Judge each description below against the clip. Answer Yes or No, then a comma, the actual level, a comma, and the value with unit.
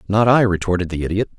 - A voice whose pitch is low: Yes, low, 100 Hz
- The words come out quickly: Yes, fast, 215 wpm